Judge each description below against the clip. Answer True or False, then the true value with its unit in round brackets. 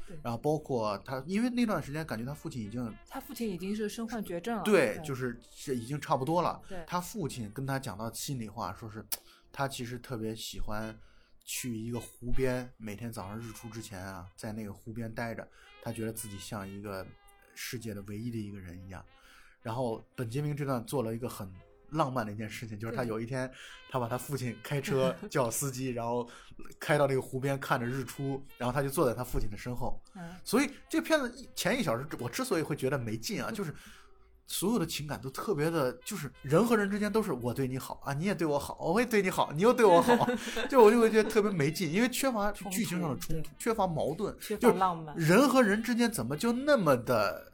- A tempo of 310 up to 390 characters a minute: True (320 characters per minute)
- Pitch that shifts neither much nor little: False (8.8 semitones)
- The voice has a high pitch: False (135 Hz)